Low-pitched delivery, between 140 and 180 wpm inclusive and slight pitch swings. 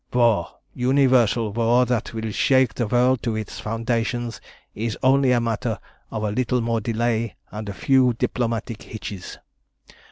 Yes: low, 115 Hz; average, 150 wpm; narrow, 2.0 semitones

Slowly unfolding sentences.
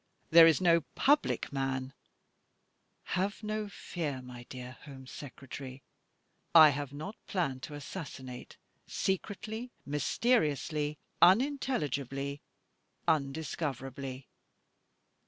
Yes: slow, 95 wpm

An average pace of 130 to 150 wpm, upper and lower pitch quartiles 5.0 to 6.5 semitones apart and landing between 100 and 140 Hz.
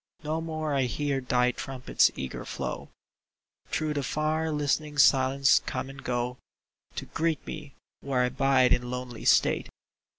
No: average, 145 wpm; average, 3.2 semitones; low, 135 Hz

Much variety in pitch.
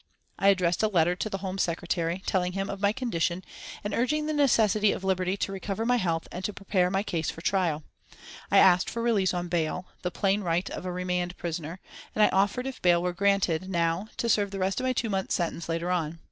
No: narrow, 2.6 semitones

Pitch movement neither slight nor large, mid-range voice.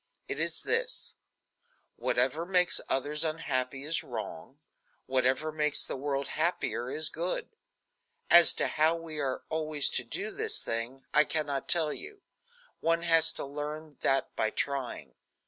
Yes: average, 3.4 semitones; medium, 155 Hz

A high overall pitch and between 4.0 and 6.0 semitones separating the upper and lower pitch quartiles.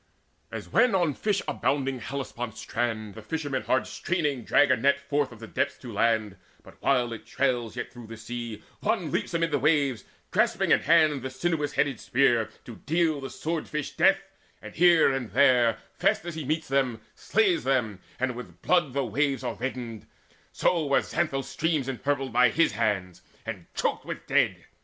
No: low, 135 Hz; average, 4.3 semitones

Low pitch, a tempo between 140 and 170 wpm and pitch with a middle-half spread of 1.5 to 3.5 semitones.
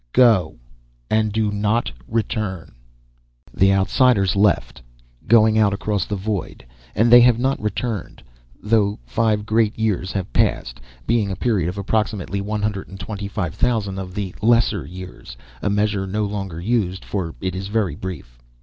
Yes: low, 100 Hz; average, 160 wpm; narrow, 2.6 semitones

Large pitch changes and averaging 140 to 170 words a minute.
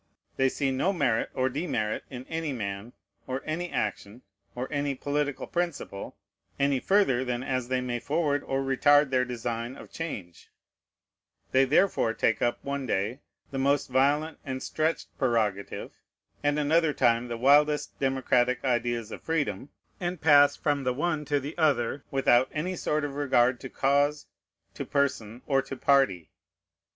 No: average, 3.0 semitones; average, 155 wpm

